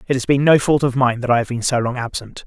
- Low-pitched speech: Yes, low, 130 Hz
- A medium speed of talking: No, fast, 340 wpm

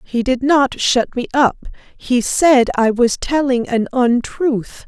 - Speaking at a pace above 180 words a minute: No, average, 160 wpm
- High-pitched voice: Yes, very high, 255 Hz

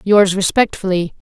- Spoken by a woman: Yes, female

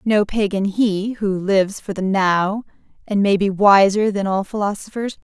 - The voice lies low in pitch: No, high, 200 Hz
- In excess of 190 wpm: No, average, 170 wpm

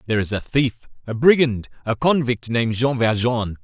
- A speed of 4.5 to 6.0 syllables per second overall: Yes, 5.4 syllables/s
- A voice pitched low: Yes, low, 120 Hz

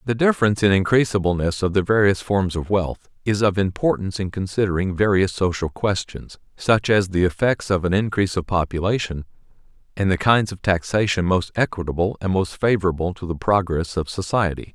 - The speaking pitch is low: Yes, very low, 95 Hz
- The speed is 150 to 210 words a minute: Yes, average, 170 wpm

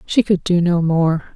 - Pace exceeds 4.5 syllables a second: No, 4.4 syllables/s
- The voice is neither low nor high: Yes, medium, 175 Hz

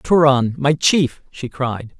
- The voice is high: No, medium, 140 Hz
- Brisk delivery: No, average, 150 wpm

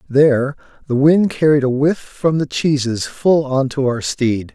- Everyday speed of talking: Yes, average, 185 wpm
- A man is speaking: Yes, male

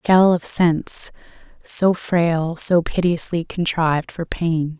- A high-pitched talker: No, medium, 170 Hz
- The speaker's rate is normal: No, slow, 125 wpm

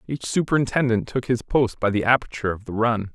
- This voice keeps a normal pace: No, fast, 210 wpm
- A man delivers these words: Yes, male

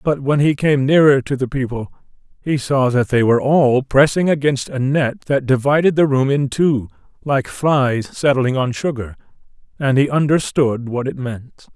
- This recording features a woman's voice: No, male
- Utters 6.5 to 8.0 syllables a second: No, 4.6 syllables/s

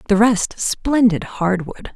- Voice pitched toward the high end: Yes, high, 210 Hz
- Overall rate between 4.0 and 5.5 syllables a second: No, 3.5 syllables/s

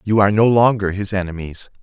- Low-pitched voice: Yes, low, 100 Hz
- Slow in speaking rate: No, average, 200 wpm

